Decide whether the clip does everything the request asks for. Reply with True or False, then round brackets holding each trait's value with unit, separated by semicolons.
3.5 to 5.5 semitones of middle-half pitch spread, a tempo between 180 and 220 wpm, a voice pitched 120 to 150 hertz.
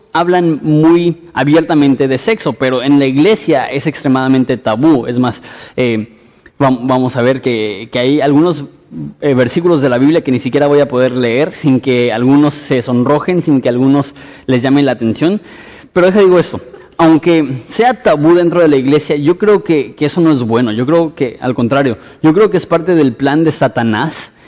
True (4.2 semitones; 190 wpm; 140 Hz)